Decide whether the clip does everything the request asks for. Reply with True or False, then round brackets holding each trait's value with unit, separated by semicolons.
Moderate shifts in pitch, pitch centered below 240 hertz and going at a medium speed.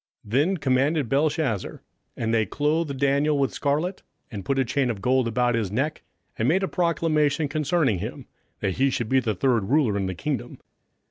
True (4.7 semitones; 135 Hz; 190 wpm)